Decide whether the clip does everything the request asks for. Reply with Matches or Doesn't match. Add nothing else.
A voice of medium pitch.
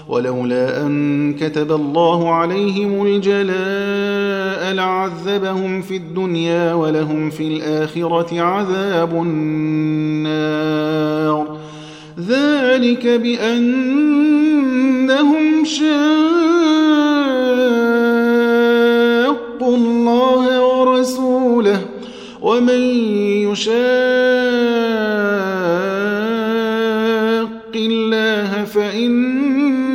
Doesn't match